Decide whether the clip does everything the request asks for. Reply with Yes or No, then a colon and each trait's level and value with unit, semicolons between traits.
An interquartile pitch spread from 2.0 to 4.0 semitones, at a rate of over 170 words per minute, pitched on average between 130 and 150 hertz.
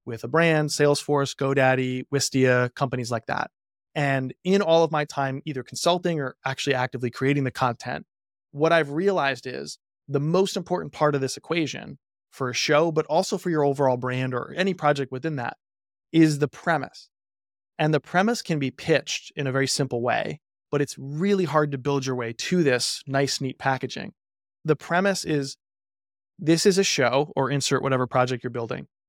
Yes: average, 3.5 semitones; average, 180 wpm; medium, 140 Hz